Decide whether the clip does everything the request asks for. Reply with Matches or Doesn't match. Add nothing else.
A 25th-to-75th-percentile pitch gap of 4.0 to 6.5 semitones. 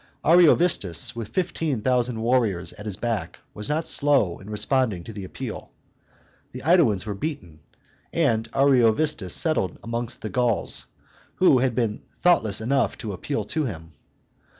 Matches